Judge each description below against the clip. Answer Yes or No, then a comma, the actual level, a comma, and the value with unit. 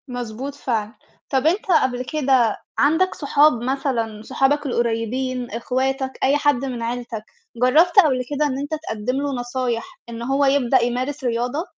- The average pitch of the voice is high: Yes, very high, 255 Hz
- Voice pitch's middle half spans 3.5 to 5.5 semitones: No, average, 2.9 semitones